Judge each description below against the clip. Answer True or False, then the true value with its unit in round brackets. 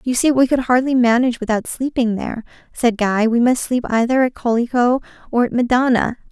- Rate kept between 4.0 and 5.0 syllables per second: False (5.7 syllables/s)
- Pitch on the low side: False (240 Hz)